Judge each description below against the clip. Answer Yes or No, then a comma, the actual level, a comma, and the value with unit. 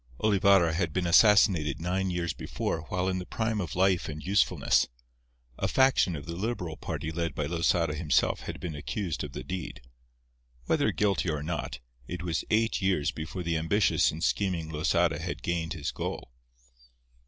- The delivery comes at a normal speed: Yes, average, 170 wpm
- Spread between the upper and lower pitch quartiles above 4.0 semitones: No, average, 3.1 semitones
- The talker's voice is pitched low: Yes, very low, 85 Hz